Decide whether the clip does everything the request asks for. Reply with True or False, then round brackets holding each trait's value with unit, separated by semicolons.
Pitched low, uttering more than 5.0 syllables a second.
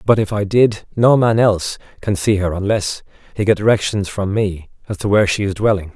True (100 Hz; 5.5 syllables/s)